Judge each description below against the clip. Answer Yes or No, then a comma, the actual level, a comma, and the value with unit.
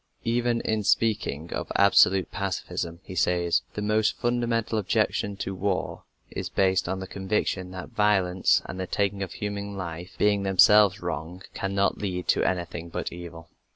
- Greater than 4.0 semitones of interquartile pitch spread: No, narrow, 2.5 semitones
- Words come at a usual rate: Yes, average, 155 wpm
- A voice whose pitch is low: Yes, very low, 95 Hz